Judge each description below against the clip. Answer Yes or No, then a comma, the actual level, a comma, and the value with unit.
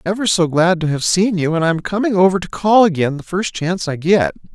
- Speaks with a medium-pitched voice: Yes, medium, 175 Hz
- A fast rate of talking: Yes, fast, 265 wpm